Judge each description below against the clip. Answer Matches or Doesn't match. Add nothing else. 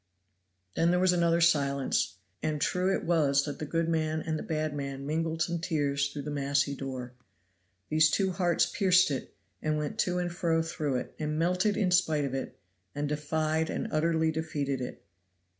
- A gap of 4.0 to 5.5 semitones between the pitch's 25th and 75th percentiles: Doesn't match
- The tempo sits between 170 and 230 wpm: Matches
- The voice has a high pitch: Doesn't match